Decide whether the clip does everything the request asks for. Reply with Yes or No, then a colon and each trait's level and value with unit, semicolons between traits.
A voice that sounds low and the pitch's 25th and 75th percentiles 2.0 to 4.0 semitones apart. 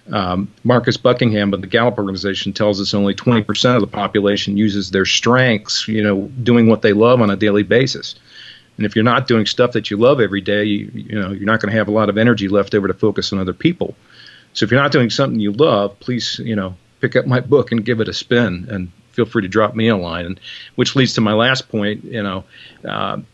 Yes: low, 105 Hz; average, 2.9 semitones